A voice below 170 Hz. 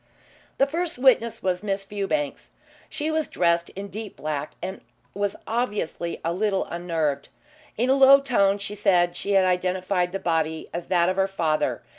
No: high, 195 Hz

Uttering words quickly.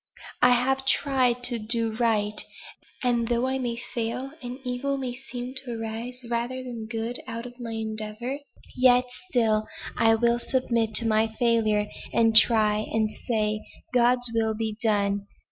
No: average, 155 wpm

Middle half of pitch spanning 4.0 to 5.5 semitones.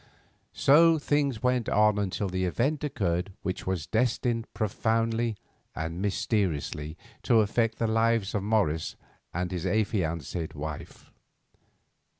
Yes: average, 4.3 semitones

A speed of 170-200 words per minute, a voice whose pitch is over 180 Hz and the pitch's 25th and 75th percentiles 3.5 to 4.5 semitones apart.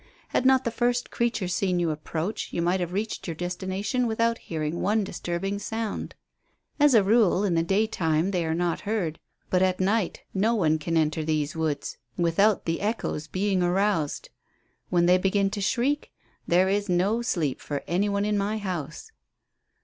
Yes: average, 175 wpm; high, 190 Hz; average, 4.0 semitones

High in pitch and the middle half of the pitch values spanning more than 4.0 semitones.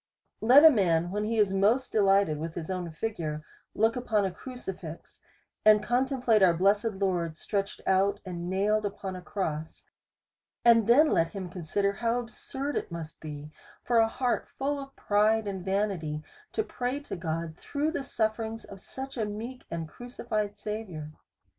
Yes: high, 205 Hz; average, 4.8 semitones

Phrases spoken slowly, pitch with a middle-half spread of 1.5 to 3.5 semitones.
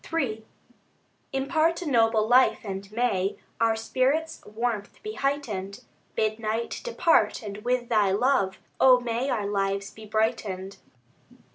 No: slow, 130 wpm; average, 4.0 semitones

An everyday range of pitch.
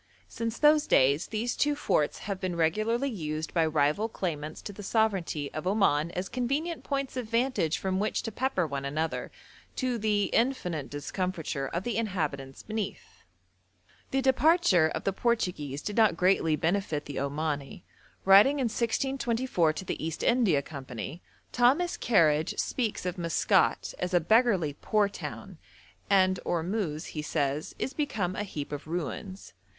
No: wide, 6.8 semitones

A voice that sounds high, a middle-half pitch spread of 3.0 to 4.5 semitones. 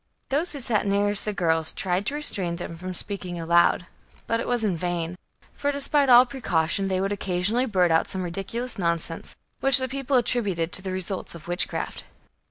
No: high, 195 Hz; wide, 5.6 semitones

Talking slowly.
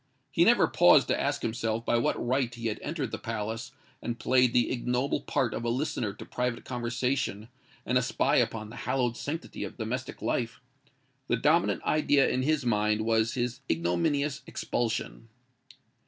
No: average, 165 wpm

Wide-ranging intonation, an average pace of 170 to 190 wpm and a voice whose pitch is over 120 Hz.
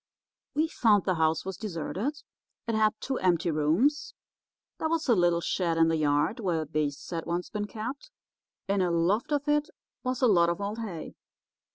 Yes: wide, 6.4 semitones; average, 185 wpm; high, 190 Hz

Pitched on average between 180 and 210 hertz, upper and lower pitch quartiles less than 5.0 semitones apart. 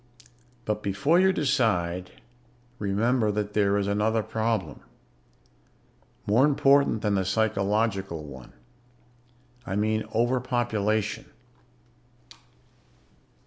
No: low, 105 Hz; average, 3.0 semitones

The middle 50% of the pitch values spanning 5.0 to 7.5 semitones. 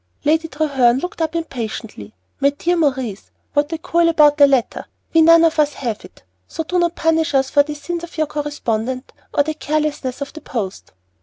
No: average, 3.6 semitones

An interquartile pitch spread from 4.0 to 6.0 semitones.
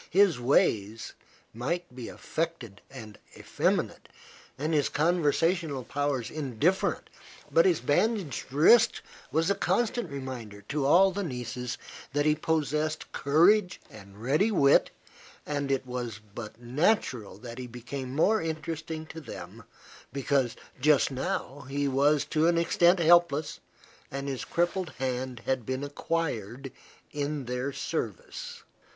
Yes: average, 4.8 semitones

